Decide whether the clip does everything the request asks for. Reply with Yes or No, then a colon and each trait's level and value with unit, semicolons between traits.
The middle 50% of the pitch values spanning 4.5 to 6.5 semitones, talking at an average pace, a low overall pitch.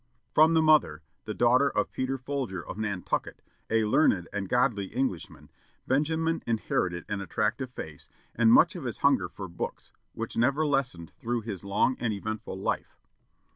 Yes: wide, 5.6 semitones; average, 160 wpm; low, 115 Hz